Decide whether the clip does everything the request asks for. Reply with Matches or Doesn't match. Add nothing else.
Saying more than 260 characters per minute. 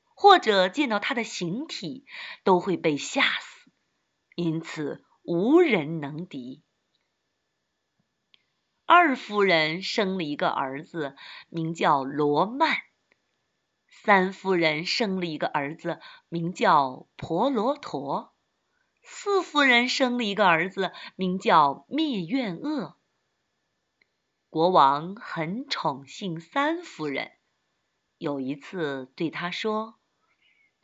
Doesn't match